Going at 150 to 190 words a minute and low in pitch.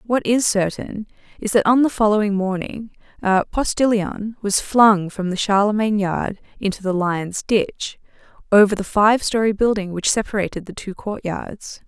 No: average, 160 wpm; high, 205 Hz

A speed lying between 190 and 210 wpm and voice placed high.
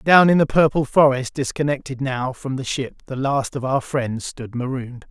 No: average, 200 wpm; low, 135 Hz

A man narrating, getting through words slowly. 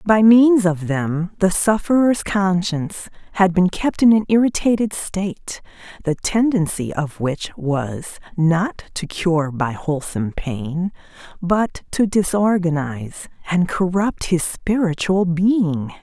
No: female; slow, 125 wpm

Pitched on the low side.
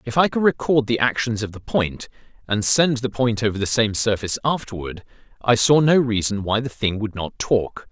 Yes: low, 115 Hz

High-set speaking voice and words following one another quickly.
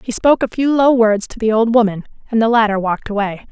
Yes: high, 225 Hz; fast, 255 wpm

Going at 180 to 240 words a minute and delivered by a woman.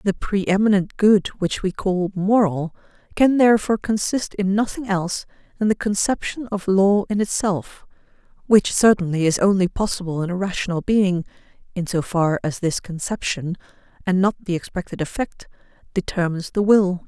No: average, 150 wpm; female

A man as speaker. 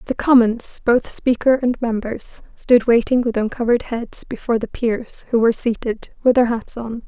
No: female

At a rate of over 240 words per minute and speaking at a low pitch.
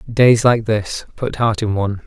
No: fast, 205 wpm; low, 110 Hz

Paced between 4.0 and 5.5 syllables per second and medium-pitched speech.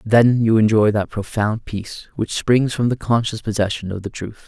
No: 4.9 syllables/s; low, 110 Hz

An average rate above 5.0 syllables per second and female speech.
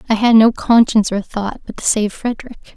Yes: 6.0 syllables/s; female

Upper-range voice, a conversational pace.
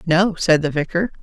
No: medium, 170 Hz; average, 195 wpm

